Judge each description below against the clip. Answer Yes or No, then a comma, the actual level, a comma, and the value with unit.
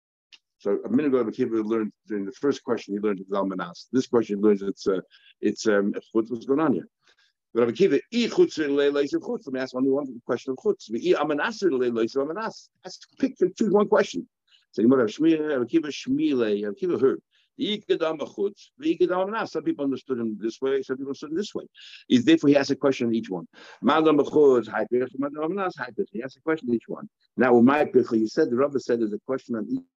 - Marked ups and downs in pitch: Yes, wide, 8.6 semitones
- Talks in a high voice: No, low, 135 Hz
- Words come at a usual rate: No, fast, 225 wpm